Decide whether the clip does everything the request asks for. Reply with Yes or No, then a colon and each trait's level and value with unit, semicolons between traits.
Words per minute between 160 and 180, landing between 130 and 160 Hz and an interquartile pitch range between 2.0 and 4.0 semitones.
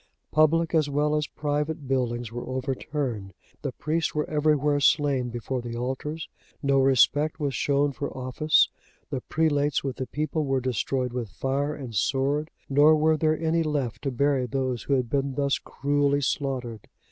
Yes: average, 165 wpm; medium, 140 Hz; average, 2.7 semitones